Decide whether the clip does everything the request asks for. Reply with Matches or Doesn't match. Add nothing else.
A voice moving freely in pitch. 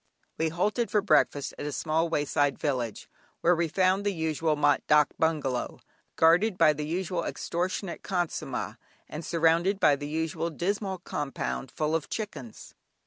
Doesn't match